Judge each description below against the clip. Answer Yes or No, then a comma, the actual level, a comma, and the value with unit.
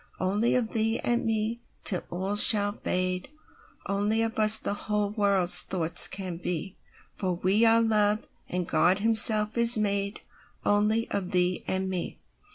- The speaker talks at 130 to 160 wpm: Yes, average, 140 wpm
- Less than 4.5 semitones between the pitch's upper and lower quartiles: Yes, average, 2.8 semitones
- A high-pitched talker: Yes, high, 205 Hz